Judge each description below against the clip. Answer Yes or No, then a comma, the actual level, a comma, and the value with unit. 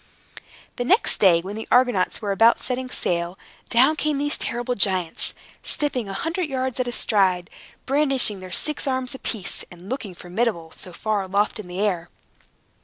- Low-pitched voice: No, high, 220 Hz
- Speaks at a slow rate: No, average, 170 wpm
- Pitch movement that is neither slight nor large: No, wide, 5.7 semitones